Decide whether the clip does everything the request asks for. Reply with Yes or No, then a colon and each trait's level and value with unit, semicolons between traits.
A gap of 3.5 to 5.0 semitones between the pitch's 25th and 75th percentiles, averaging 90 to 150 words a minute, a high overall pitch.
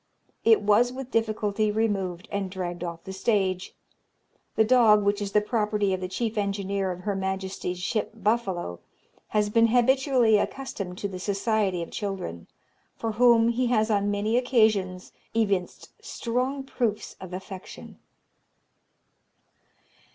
No: average, 3.1 semitones; slow, 135 wpm; high, 205 Hz